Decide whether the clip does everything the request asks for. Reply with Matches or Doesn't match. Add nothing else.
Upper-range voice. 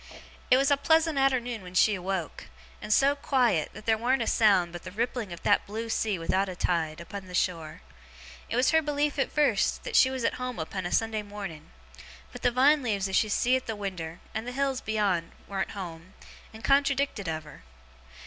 Matches